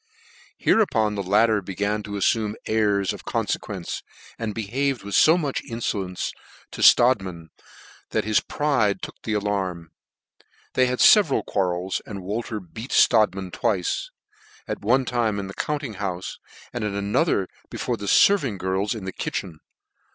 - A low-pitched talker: Yes, low, 105 Hz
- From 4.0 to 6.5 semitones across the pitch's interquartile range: No, average, 3.5 semitones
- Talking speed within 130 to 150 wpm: Yes, average, 145 wpm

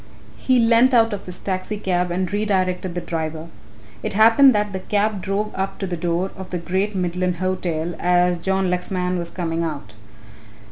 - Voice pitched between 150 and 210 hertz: Yes, medium, 185 Hz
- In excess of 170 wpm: Yes, average, 180 wpm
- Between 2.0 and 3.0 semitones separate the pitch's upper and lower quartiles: Yes, narrow, 2.5 semitones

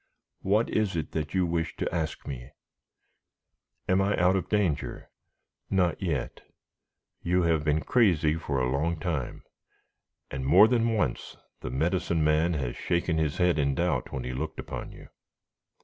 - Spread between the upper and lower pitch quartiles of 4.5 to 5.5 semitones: No, average, 3.8 semitones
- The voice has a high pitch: No, very low, 80 Hz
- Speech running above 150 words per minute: Yes, average, 160 wpm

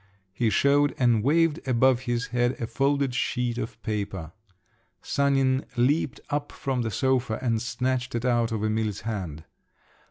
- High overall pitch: No, low, 120 Hz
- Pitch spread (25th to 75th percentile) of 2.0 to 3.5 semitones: Yes, average, 3.0 semitones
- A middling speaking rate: Yes, average, 150 wpm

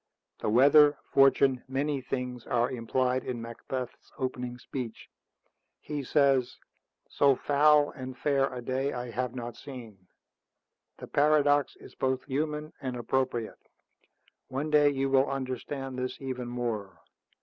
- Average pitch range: No, narrow, 2.2 semitones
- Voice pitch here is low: Yes, low, 130 Hz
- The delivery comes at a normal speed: No, slow, 130 wpm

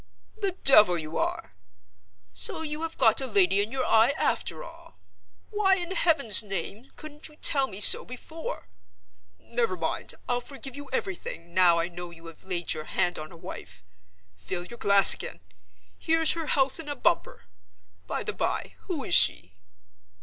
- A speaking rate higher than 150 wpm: Yes, average, 170 wpm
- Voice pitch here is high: Yes, high, 235 Hz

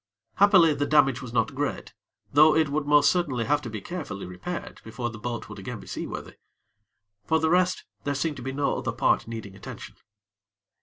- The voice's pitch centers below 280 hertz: Yes, medium, 140 Hz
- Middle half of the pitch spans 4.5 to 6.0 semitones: Yes, average, 5.2 semitones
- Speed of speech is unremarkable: Yes, average, 195 wpm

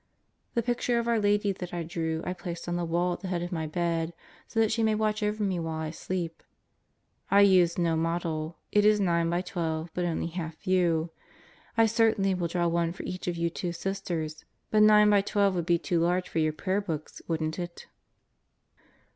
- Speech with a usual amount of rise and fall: Yes, average, 3.3 semitones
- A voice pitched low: No, medium, 175 Hz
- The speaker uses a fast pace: Yes, fast, 210 wpm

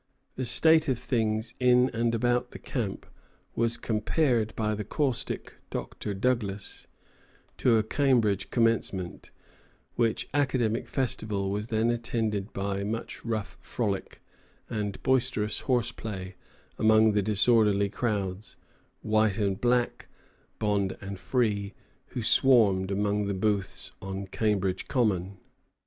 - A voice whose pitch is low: Yes, low, 110 Hz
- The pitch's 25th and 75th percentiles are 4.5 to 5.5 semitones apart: No, average, 3.1 semitones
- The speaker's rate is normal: No, slow, 120 wpm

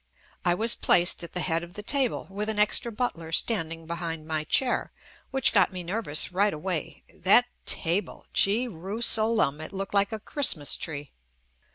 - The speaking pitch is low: No, high, 190 Hz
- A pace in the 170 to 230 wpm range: Yes, average, 175 wpm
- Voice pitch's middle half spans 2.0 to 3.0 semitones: No, average, 5.0 semitones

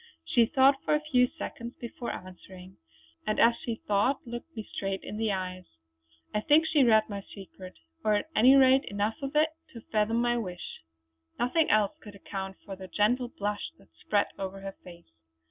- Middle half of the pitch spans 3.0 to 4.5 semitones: Yes, average, 4.2 semitones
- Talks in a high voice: Yes, high, 215 Hz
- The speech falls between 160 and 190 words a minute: Yes, average, 185 wpm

